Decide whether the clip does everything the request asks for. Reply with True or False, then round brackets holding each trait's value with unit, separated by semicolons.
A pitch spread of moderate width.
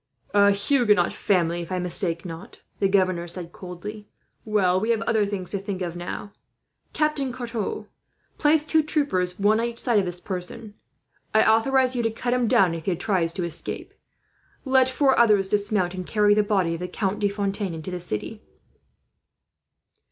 True (4.1 semitones)